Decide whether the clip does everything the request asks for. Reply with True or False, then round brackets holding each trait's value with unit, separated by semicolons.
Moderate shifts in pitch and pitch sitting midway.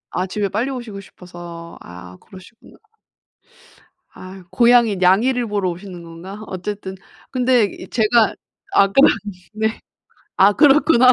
False (4.5 semitones; 200 Hz)